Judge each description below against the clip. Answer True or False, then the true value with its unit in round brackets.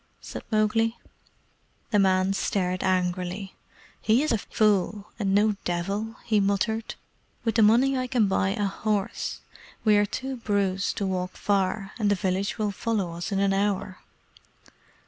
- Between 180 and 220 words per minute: False (155 wpm)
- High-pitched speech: True (200 Hz)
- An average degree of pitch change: False (2.3 semitones)